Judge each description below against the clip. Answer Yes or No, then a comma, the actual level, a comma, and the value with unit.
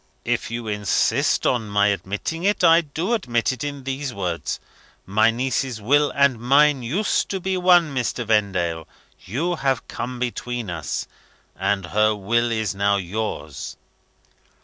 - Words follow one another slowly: No, average, 150 wpm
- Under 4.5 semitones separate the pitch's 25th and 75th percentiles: No, wide, 5.6 semitones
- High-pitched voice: No, low, 120 Hz